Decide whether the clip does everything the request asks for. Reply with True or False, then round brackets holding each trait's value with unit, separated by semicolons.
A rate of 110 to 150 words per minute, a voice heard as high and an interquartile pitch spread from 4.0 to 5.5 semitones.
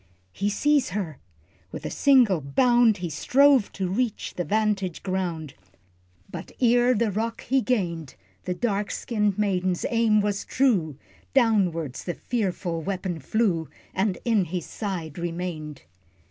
True (135 wpm; 200 Hz; 4.8 semitones)